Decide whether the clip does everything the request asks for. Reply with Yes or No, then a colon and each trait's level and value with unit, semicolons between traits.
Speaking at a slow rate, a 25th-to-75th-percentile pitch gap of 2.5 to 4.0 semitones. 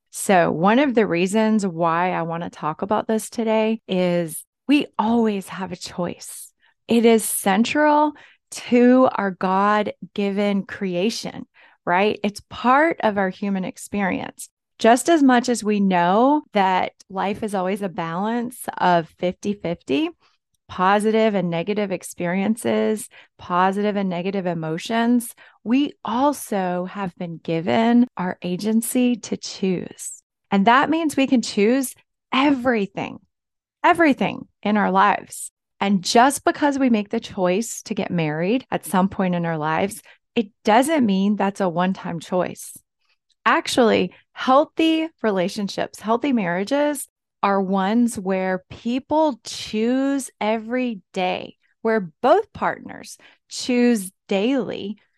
No: slow, 130 wpm; average, 4.6 semitones